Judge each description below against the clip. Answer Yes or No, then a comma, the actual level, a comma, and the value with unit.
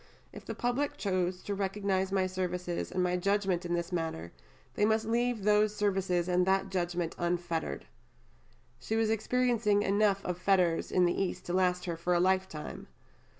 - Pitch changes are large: No, average, 2.7 semitones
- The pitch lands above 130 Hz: Yes, medium, 185 Hz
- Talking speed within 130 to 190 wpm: Yes, average, 170 wpm